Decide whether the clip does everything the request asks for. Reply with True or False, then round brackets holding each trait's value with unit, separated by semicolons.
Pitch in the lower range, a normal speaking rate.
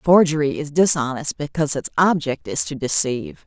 False (150 Hz; 155 wpm)